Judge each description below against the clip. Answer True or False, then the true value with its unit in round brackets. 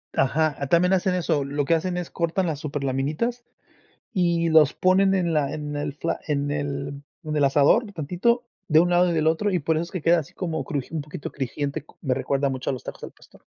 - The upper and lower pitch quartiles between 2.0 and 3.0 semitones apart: False (3.8 semitones)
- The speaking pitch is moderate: True (155 Hz)